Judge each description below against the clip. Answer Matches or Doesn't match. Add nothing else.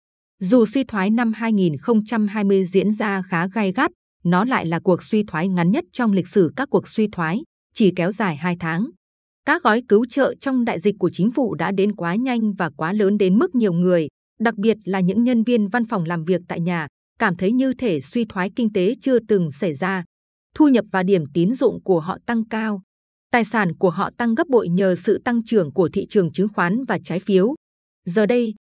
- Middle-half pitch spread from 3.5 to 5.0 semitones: Matches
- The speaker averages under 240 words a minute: Matches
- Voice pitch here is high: Matches